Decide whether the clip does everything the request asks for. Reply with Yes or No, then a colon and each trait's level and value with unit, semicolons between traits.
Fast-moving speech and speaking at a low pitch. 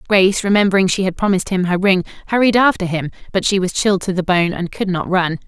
No: fast, 240 wpm; high, 190 Hz